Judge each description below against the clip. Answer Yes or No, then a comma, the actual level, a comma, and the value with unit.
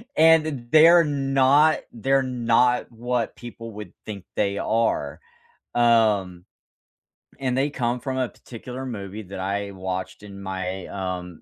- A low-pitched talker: Yes, low, 115 Hz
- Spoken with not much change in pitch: No, average, 5.0 semitones